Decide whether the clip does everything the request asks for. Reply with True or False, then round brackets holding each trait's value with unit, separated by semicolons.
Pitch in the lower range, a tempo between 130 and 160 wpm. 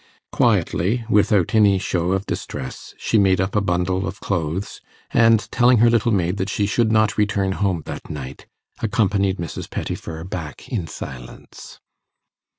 True (95 Hz; 155 wpm)